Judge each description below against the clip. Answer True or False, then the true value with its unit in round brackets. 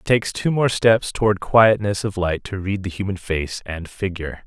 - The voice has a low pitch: True (100 Hz)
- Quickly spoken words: True (215 wpm)